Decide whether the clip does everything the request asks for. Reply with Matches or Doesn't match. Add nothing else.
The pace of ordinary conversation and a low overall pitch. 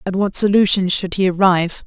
Doesn't match